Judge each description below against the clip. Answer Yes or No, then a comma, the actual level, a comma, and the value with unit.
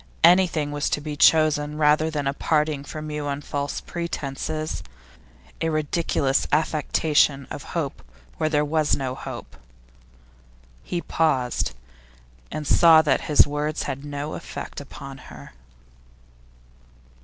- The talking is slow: Yes, slow, 125 wpm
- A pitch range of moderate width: No, narrow, 1.7 semitones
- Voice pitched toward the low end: No, medium, 150 Hz